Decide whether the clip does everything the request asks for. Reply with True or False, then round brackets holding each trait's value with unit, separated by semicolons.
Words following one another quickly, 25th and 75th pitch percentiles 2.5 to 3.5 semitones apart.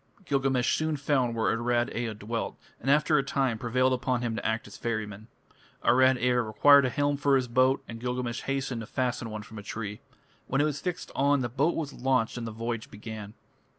True (210 wpm; 3.1 semitones)